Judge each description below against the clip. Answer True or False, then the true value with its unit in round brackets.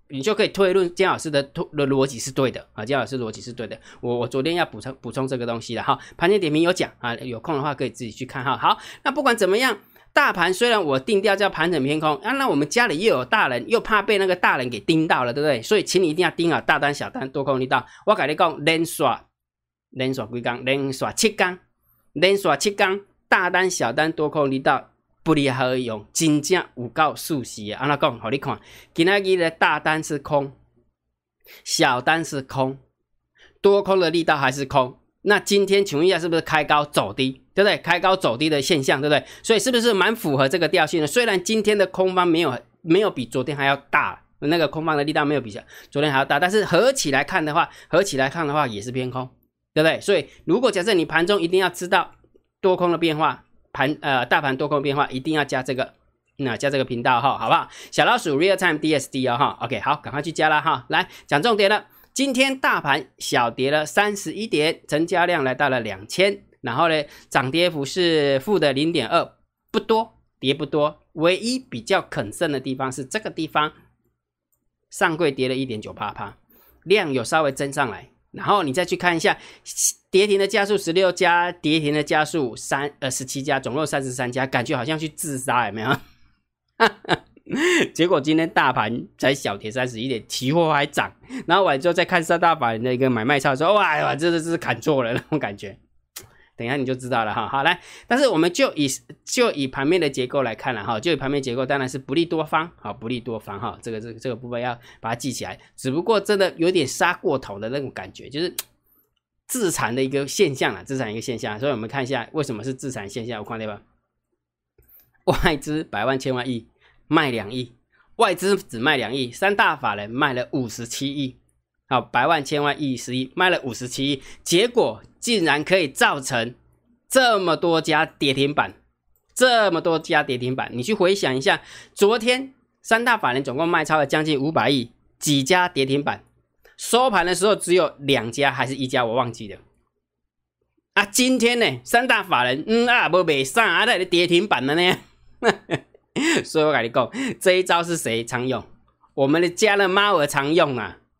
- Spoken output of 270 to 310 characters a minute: True (305 characters per minute)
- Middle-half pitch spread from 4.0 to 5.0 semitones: False (5.6 semitones)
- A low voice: False (145 Hz)